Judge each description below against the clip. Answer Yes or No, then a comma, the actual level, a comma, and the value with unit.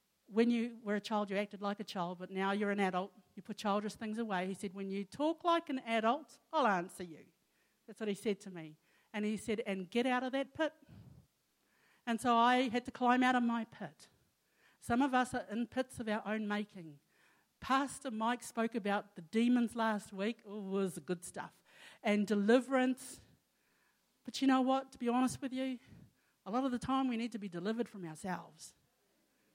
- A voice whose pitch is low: No, high, 225 Hz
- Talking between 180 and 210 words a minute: Yes, fast, 205 wpm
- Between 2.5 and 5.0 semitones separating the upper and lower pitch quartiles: Yes, average, 3.7 semitones